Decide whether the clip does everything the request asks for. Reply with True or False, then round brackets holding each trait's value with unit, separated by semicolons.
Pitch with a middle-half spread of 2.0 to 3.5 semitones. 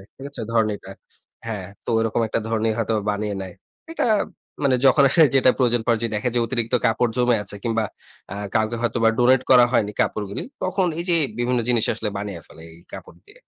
True (2.7 semitones)